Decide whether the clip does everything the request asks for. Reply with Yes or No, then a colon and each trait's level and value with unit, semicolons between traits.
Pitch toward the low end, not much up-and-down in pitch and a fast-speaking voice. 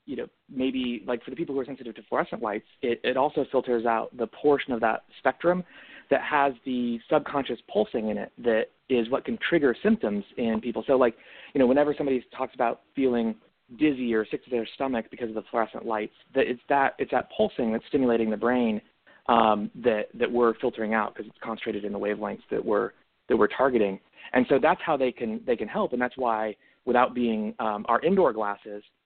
No: low, 120 Hz; average, 3.3 semitones; fast, 215 wpm